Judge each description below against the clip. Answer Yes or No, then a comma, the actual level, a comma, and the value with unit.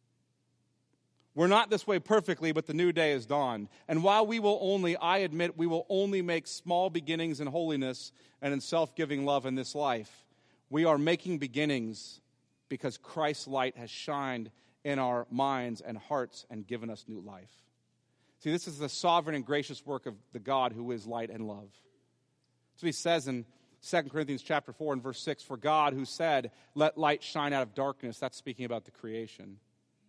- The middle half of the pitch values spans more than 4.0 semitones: Yes, average, 4.8 semitones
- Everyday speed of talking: Yes, average, 185 wpm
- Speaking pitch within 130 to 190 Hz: Yes, medium, 140 Hz